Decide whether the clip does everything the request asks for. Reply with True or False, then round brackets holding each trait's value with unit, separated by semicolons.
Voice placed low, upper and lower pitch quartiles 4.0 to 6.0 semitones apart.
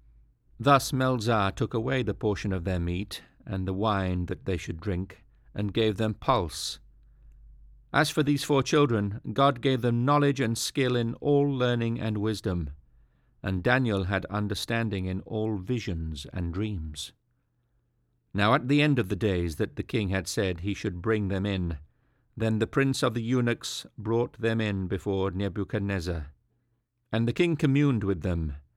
True (110 Hz; 4.3 semitones)